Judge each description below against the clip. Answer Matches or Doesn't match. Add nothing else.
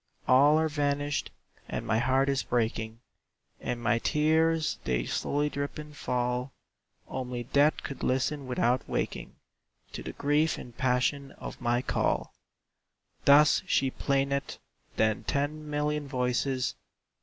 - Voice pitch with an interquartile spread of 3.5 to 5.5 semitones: Doesn't match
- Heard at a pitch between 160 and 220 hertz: Doesn't match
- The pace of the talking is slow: Matches